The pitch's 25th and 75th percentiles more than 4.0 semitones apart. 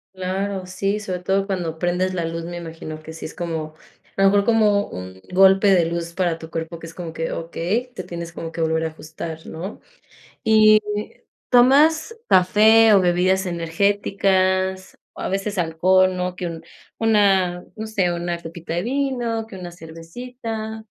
No: average, 3.5 semitones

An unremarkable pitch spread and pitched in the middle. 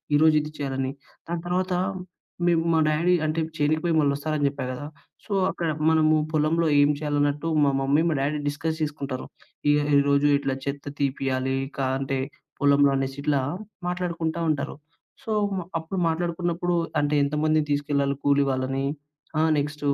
No: narrow, 2.3 semitones; medium, 145 Hz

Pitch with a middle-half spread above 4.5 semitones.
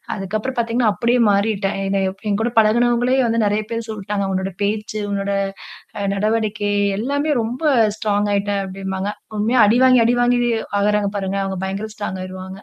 No: average, 2.8 semitones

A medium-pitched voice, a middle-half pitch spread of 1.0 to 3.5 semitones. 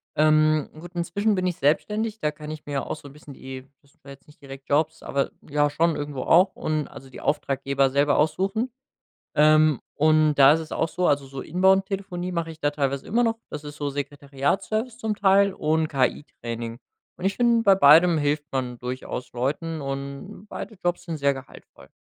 No: medium, 155 Hz; average, 4.4 semitones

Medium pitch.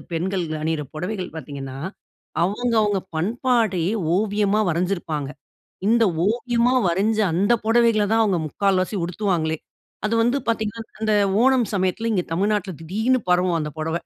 No: high, 200 Hz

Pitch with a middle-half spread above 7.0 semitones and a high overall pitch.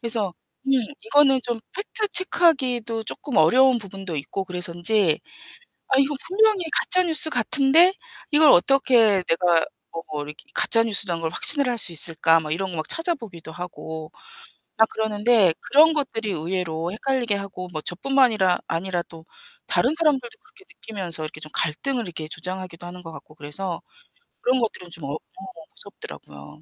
Yes: wide, 8.0 semitones; high, 200 Hz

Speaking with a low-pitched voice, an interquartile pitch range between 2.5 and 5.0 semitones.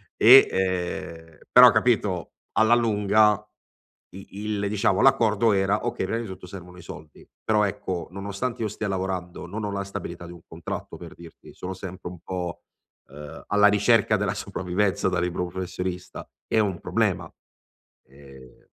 Yes: very low, 95 Hz; average, 2.8 semitones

